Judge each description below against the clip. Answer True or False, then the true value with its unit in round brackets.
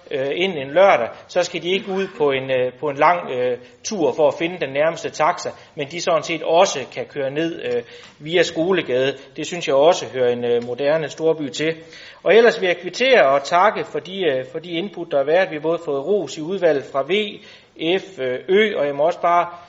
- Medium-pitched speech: True (160 Hz)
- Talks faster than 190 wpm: True (225 wpm)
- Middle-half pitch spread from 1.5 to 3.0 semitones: False (4.4 semitones)